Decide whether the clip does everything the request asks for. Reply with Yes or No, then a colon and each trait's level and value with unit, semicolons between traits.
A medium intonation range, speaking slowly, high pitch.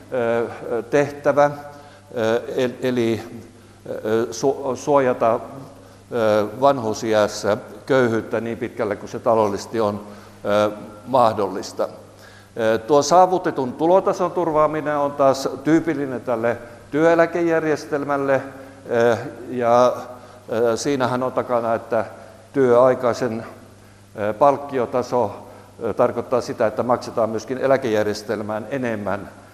No: average, 4.0 semitones; slow, 70 wpm; low, 120 Hz